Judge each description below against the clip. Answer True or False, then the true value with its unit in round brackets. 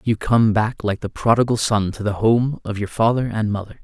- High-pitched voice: False (110 Hz)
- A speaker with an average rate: False (235 wpm)